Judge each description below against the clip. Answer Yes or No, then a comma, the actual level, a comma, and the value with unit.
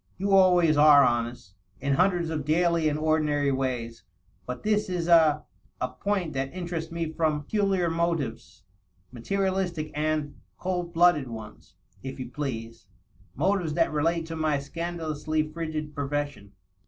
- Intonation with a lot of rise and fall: No, average, 3.9 semitones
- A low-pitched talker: No, medium, 155 Hz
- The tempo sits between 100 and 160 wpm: Yes, average, 150 wpm